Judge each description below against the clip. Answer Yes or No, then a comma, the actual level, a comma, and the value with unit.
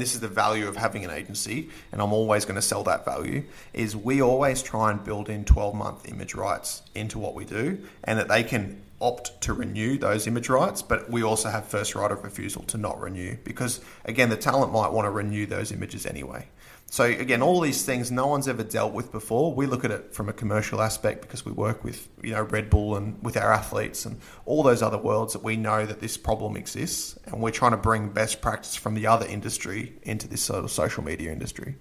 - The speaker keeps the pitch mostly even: Yes, narrow, 2.3 semitones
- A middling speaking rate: No, fast, 235 wpm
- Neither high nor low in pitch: No, low, 110 Hz